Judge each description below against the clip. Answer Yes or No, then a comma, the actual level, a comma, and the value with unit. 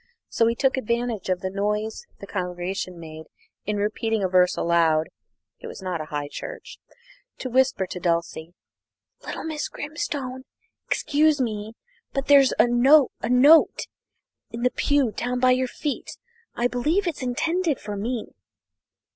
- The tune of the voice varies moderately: No, wide, 6.1 semitones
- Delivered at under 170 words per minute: Yes, average, 150 wpm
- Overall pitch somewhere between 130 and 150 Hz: No, high, 235 Hz